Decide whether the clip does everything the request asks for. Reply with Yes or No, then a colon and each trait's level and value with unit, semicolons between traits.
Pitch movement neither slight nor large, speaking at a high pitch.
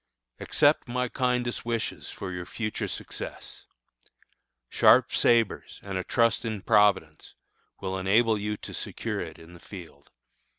No: average, 3.9 semitones; low, 105 Hz